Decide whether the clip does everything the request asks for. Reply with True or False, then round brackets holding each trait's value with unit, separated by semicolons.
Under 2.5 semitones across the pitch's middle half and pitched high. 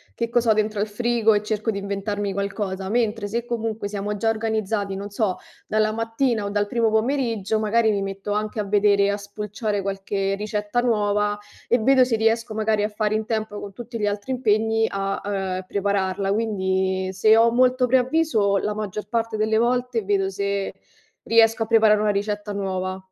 True (2.0 semitones; 210 Hz)